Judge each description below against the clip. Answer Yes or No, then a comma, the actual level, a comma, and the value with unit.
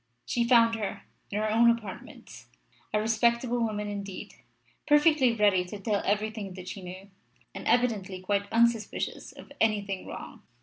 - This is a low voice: No, high, 215 Hz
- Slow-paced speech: No, average, 145 wpm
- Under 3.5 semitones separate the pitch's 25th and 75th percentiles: Yes, average, 2.8 semitones